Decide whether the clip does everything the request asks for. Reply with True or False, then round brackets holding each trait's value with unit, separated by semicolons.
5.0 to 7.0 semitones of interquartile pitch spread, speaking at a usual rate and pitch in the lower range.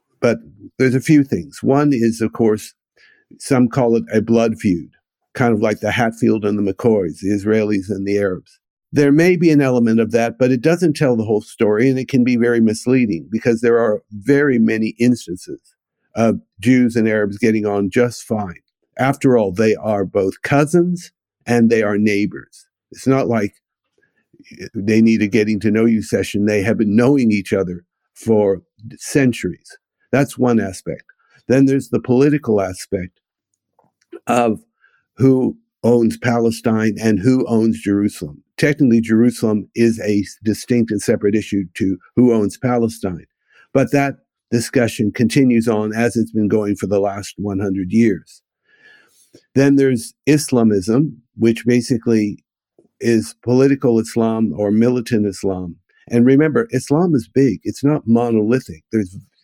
False (3.4 semitones; 155 wpm; 115 Hz)